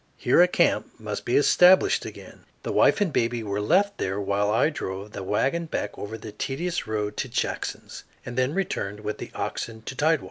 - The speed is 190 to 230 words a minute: Yes, average, 200 wpm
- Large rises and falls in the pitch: Yes, wide, 7.8 semitones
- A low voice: Yes, low, 115 Hz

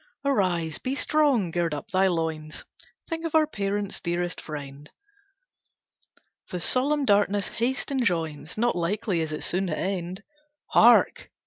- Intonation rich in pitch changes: Yes, wide, 6.4 semitones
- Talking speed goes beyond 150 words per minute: No, slow, 135 wpm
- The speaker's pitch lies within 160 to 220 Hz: Yes, high, 190 Hz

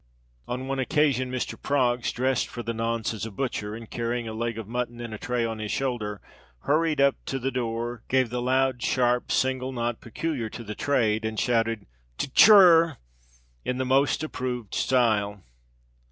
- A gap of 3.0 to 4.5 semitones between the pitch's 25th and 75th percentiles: No, narrow, 2.5 semitones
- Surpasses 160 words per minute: Yes, average, 180 wpm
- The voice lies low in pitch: Yes, low, 120 Hz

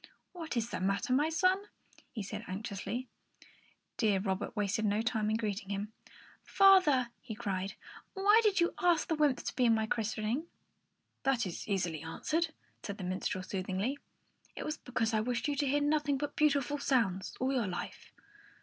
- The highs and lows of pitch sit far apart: Yes, wide, 6.4 semitones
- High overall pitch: Yes, high, 235 Hz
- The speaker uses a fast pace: No, average, 170 wpm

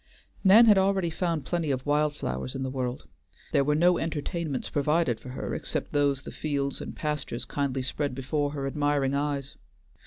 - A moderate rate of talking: Yes, average, 180 wpm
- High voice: No, medium, 145 Hz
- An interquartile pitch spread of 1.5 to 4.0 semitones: Yes, average, 2.8 semitones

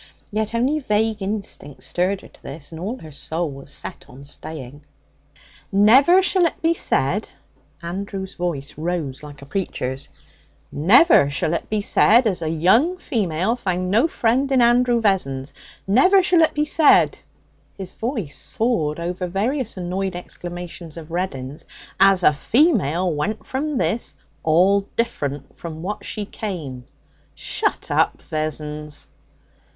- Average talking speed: Yes, average, 145 wpm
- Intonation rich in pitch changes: Yes, wide, 6.8 semitones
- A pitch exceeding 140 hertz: Yes, medium, 185 Hz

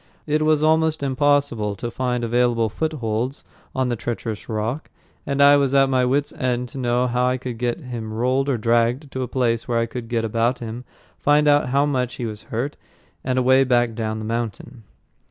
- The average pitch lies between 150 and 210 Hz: No, low, 125 Hz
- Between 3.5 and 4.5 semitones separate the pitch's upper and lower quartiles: No, average, 2.8 semitones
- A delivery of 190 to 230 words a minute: Yes, average, 200 wpm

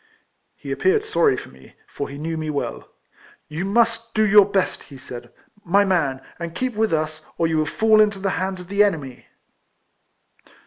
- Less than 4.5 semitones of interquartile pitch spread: No, wide, 5.4 semitones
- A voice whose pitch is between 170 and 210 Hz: Yes, high, 190 Hz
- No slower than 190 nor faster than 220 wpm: Yes, average, 195 wpm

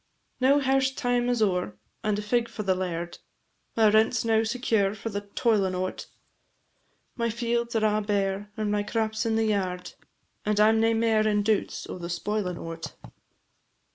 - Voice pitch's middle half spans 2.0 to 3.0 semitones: Yes, narrow, 2.5 semitones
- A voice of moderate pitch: No, high, 215 Hz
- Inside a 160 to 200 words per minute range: Yes, average, 185 wpm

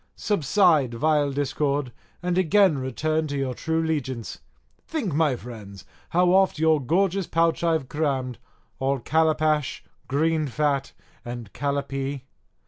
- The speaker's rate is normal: No, slow, 125 wpm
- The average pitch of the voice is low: No, medium, 150 Hz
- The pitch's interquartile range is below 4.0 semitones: Yes, average, 3.4 semitones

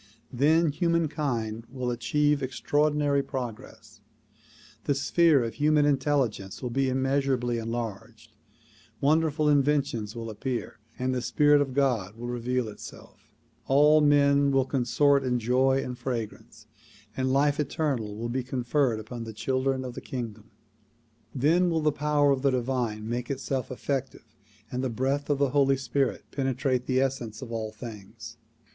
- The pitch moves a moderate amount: Yes, average, 3.1 semitones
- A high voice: No, low, 130 Hz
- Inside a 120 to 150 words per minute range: Yes, average, 145 wpm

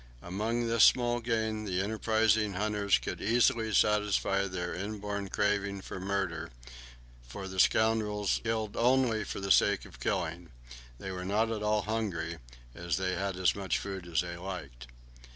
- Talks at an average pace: Yes, average, 155 wpm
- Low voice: Yes, low, 100 Hz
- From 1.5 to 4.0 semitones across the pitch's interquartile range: Yes, average, 3.0 semitones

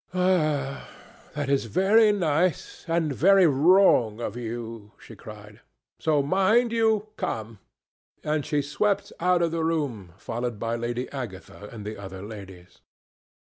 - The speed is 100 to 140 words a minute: Yes, slow, 135 wpm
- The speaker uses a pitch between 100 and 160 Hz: Yes, medium, 140 Hz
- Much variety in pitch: Yes, wide, 7.9 semitones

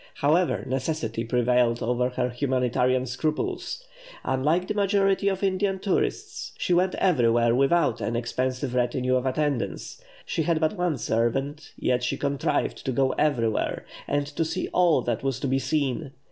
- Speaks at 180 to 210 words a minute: No, average, 155 wpm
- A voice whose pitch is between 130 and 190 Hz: Yes, low, 135 Hz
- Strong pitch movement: No, average, 4.6 semitones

